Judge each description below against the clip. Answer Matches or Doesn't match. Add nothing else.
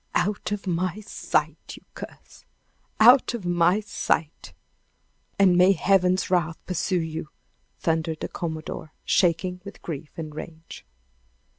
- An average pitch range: Matches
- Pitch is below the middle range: Doesn't match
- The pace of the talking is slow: Matches